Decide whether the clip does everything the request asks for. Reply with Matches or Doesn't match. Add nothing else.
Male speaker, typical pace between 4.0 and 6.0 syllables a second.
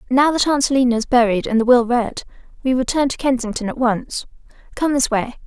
Doesn't match